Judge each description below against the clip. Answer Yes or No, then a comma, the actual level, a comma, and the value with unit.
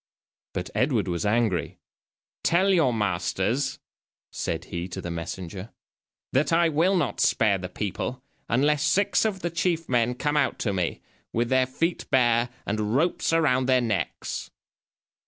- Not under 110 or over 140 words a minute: No, average, 150 wpm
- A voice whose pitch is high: No, low, 125 Hz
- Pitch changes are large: Yes, wide, 6.6 semitones